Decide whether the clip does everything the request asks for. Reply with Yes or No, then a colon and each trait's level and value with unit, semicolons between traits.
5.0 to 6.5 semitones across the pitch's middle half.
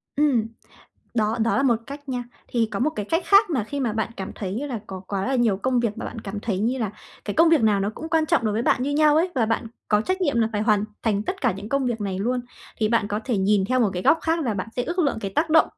Yes: average, 5.3 semitones